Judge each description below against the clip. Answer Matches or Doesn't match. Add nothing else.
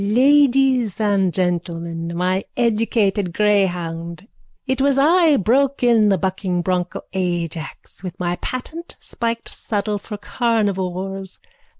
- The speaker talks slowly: Matches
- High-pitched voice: Matches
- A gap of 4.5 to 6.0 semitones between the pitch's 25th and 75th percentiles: Matches